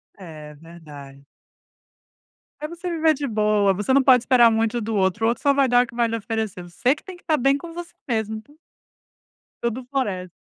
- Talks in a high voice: Yes, high, 230 Hz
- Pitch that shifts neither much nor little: No, wide, 5.7 semitones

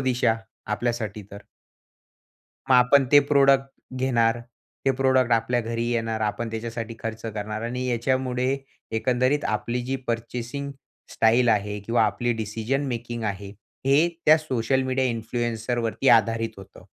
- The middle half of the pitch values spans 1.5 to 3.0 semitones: Yes, narrow, 2.4 semitones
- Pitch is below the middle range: Yes, low, 120 Hz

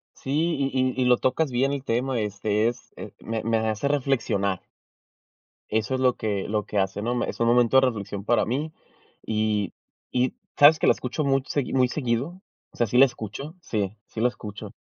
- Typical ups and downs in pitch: Yes, average, 3.7 semitones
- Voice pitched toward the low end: Yes, low, 120 Hz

